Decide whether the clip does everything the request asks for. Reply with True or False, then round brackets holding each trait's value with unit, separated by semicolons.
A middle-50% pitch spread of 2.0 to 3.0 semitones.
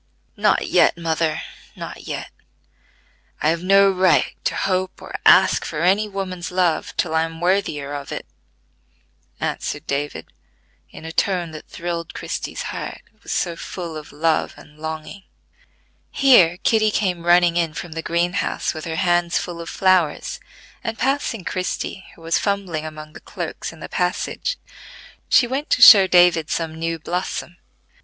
True (2.7 semitones)